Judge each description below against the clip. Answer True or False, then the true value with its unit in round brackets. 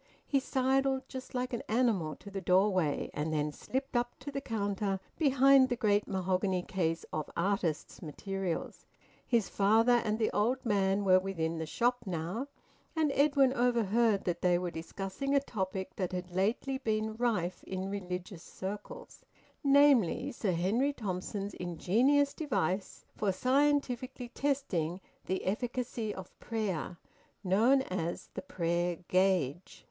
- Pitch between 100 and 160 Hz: False (205 Hz)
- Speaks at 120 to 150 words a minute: True (140 wpm)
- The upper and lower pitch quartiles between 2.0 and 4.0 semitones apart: False (5.6 semitones)